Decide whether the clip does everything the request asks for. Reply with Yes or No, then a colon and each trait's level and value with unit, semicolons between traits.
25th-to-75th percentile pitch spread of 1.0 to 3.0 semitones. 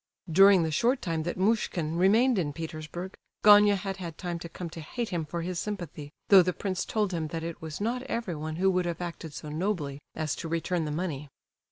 No: average, 3.5 semitones